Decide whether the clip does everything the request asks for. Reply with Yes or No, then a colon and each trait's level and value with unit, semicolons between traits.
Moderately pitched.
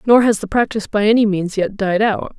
No: high, 210 Hz